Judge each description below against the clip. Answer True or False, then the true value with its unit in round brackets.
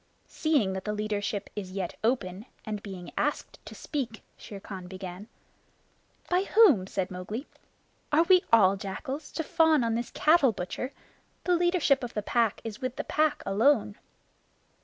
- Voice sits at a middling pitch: False (225 Hz)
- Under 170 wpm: True (160 wpm)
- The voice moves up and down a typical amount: False (7.1 semitones)